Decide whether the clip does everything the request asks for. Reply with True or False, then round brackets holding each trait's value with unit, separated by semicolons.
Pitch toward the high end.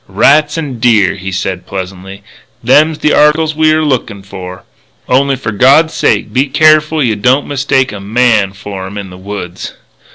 False (120 Hz)